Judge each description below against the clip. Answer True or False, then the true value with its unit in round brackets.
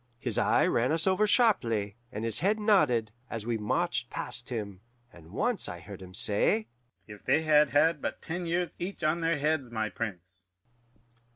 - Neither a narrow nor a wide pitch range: False (7.9 semitones)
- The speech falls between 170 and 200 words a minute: True (180 wpm)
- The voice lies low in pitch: True (125 Hz)